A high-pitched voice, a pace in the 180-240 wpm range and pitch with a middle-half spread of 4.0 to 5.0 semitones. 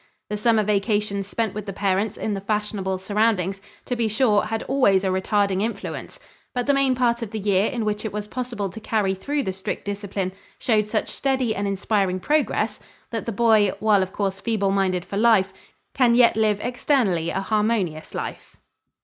No: high, 210 Hz; average, 190 wpm; average, 2.8 semitones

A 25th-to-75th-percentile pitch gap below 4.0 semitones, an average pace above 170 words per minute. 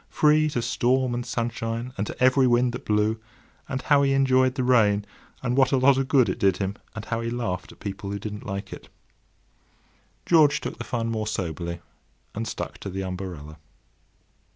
No: average, 4.3 semitones; average, 190 wpm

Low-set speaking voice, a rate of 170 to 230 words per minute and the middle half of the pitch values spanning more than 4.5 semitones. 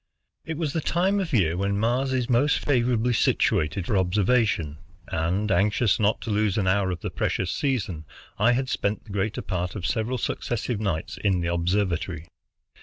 Yes: low, 105 Hz; average, 180 wpm; average, 5.1 semitones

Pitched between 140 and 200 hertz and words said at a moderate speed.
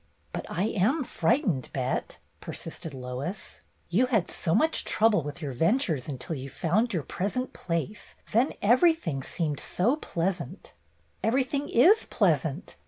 Yes: high, 190 Hz; average, 150 wpm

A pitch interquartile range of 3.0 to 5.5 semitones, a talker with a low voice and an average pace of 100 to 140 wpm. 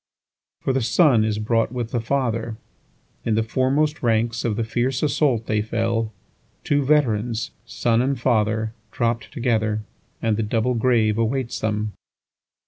No: narrow, 2.5 semitones; low, 115 Hz; slow, 135 wpm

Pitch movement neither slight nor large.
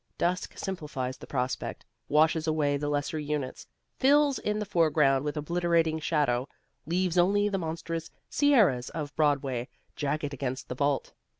Yes: average, 3.6 semitones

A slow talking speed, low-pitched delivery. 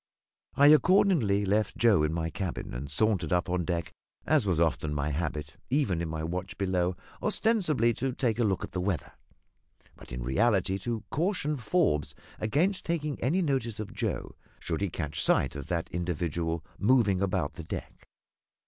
No: average, 170 wpm; very low, 95 Hz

